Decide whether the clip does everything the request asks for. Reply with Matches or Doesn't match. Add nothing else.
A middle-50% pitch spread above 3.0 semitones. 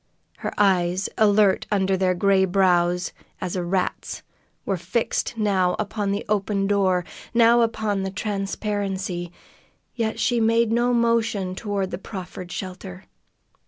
Doesn't match